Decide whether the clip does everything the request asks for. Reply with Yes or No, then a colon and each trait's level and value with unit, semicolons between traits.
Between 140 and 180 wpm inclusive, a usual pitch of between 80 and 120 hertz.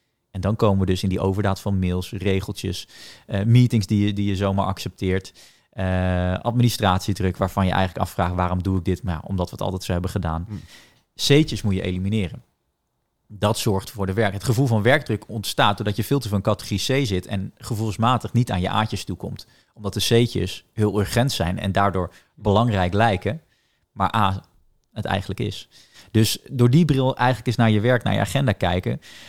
No: average, 195 wpm; low, 100 Hz